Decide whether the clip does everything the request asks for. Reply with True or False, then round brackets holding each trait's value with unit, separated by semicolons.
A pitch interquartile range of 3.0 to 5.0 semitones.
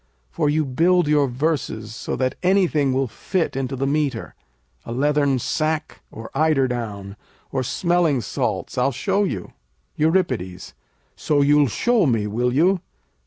True (4.3 semitones)